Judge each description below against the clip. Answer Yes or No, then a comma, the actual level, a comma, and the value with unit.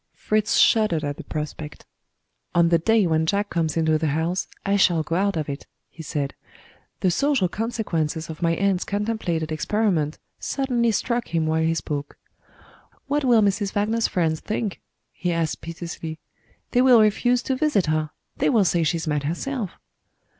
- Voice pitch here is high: No, medium, 175 Hz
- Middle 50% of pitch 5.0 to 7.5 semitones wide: Yes, average, 5.3 semitones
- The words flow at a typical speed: Yes, average, 170 wpm